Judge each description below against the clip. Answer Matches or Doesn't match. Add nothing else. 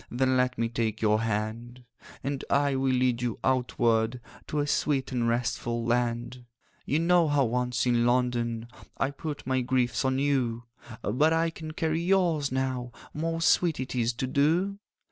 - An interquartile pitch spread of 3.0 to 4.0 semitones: Matches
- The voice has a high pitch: Doesn't match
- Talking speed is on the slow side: Doesn't match